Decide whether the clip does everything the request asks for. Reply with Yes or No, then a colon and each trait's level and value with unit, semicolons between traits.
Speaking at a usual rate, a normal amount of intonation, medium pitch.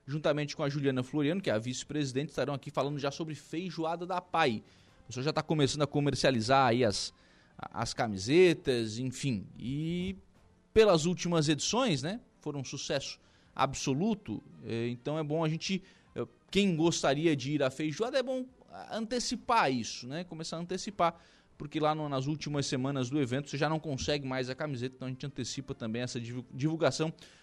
Yes: average, 170 wpm; average, 4.0 semitones; medium, 145 Hz